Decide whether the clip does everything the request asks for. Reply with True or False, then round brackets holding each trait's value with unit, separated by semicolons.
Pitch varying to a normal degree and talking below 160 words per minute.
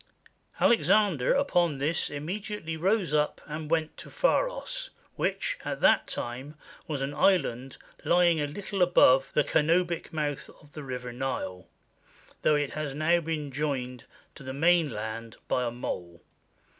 True (4.5 semitones; 145 wpm)